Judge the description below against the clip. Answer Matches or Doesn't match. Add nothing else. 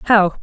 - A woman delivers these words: Matches